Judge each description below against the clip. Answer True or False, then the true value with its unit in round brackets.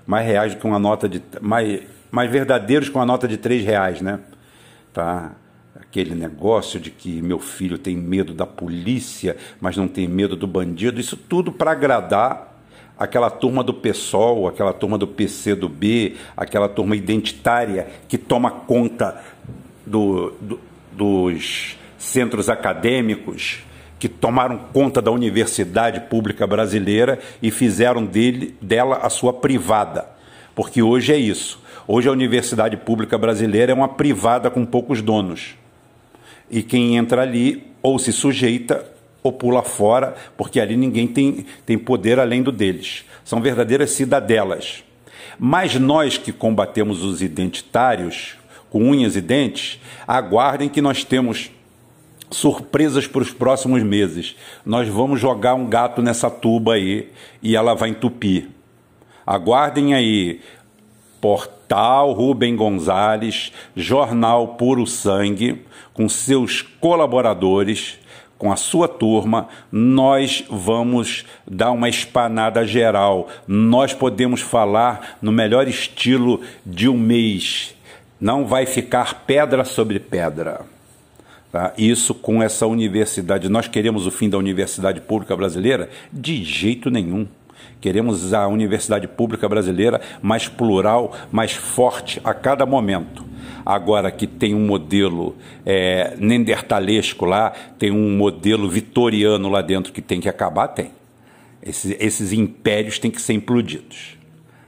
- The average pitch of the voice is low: True (115 Hz)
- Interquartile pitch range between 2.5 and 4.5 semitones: True (3.3 semitones)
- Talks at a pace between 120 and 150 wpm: True (130 wpm)